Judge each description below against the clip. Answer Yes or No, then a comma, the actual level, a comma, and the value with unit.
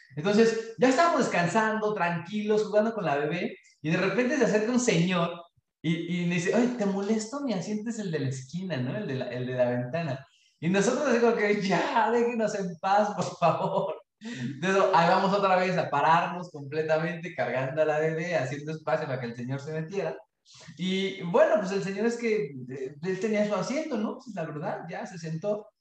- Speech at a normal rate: No, fast, 200 wpm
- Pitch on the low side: No, medium, 185 Hz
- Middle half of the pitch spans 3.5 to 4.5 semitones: No, average, 5.2 semitones